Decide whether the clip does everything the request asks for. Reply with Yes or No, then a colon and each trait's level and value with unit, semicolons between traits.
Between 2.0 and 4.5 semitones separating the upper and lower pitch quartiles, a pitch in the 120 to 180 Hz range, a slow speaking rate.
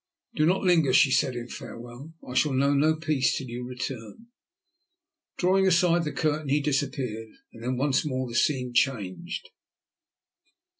No: average, 3.8 semitones; low, 135 Hz; average, 155 wpm